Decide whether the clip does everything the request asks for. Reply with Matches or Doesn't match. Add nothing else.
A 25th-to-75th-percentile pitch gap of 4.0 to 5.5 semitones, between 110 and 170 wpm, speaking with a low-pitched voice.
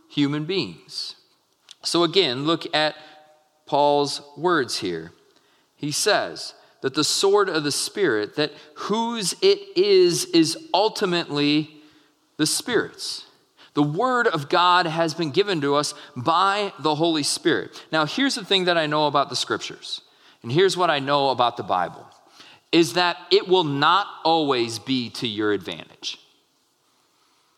Doesn't match